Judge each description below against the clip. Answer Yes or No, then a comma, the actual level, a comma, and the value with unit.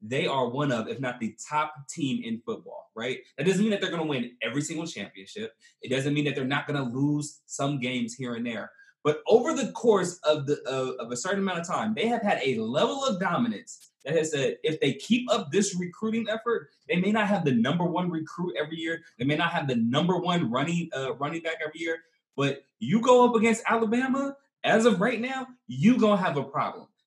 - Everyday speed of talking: No, fast, 235 wpm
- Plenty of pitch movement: Yes, wide, 7.6 semitones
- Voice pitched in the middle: Yes, medium, 175 Hz